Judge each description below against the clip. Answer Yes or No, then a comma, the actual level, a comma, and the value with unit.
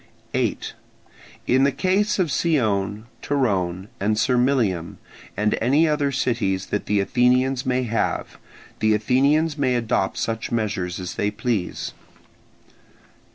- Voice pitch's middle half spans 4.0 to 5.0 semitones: Yes, average, 4.7 semitones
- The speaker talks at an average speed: No, slow, 120 wpm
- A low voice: Yes, low, 120 Hz